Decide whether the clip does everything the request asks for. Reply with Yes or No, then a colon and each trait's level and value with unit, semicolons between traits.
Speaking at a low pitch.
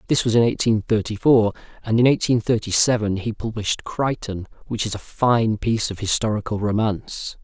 Yes: low, 110 Hz